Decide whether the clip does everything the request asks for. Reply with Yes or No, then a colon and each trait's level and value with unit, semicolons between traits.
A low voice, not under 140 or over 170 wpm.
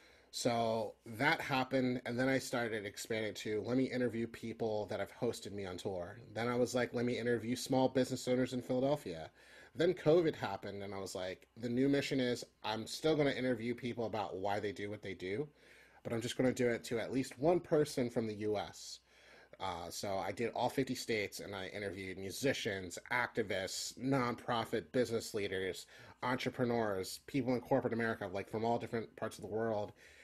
No: low, 120 Hz; average, 190 wpm